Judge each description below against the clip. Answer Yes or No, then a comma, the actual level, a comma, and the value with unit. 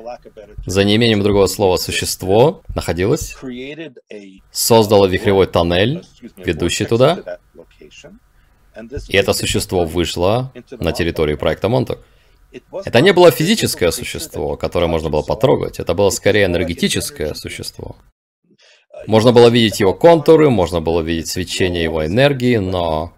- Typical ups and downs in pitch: No, wide, 6.0 semitones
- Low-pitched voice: Yes, low, 105 Hz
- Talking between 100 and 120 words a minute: Yes, average, 115 wpm